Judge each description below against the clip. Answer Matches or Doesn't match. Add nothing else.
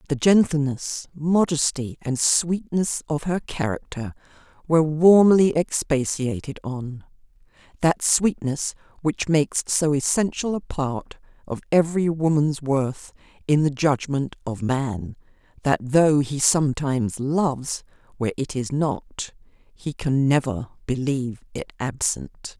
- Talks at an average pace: Doesn't match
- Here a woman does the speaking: Matches